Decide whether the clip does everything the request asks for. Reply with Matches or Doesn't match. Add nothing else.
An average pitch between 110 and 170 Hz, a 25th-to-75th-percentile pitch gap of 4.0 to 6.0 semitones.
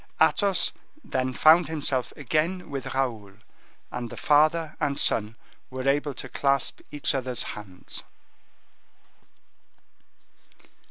Doesn't match